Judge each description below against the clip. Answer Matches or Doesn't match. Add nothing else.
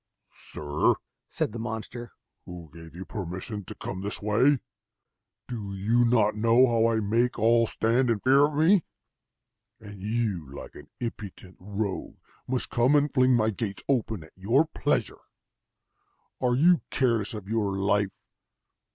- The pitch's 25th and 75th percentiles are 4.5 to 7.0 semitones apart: Doesn't match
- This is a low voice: Matches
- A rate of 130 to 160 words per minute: Matches